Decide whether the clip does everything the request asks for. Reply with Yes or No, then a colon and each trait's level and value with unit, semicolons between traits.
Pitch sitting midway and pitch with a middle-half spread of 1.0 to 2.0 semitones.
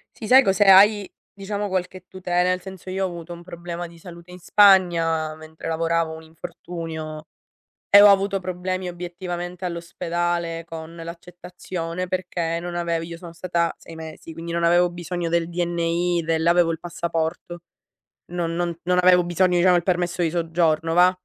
Yes: medium, 175 Hz; narrow, 1.4 semitones